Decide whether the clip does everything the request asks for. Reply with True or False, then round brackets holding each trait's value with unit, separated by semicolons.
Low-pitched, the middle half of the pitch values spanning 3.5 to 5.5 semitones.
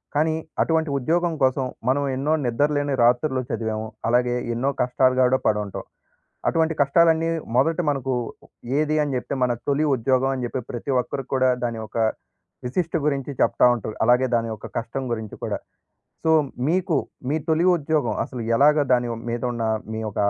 True (130 Hz; 3.9 semitones)